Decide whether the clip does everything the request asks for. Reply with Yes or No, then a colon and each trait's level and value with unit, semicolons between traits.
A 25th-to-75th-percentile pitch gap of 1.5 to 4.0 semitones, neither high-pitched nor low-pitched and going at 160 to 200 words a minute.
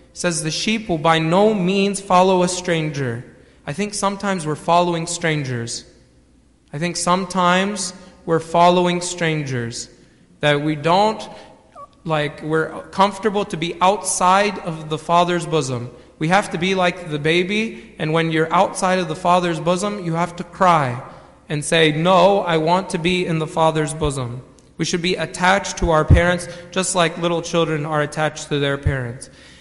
Yes: average, 2.9 semitones; medium, 170 Hz; average, 165 wpm